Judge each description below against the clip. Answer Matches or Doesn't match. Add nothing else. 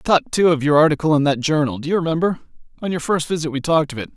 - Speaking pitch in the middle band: Matches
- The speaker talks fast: Matches